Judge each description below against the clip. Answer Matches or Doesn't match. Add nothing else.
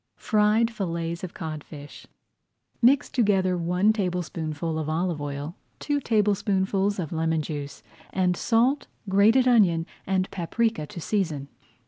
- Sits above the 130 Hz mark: Matches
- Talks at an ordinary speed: Doesn't match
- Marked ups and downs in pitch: Doesn't match